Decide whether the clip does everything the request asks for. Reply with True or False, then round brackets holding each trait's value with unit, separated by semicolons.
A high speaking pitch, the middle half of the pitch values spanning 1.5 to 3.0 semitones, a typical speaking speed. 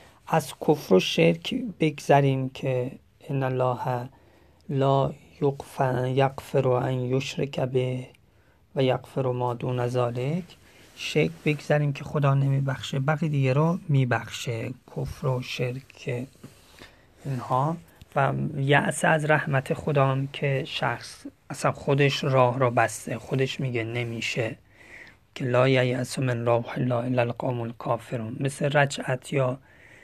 False (130 Hz; 2.4 semitones; 120 wpm)